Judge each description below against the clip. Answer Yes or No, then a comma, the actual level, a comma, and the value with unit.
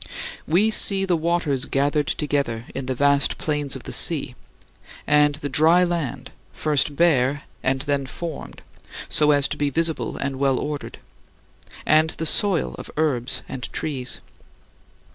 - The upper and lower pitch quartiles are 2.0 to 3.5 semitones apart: Yes, average, 2.7 semitones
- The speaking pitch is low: No, medium, 145 Hz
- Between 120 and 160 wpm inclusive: Yes, average, 145 wpm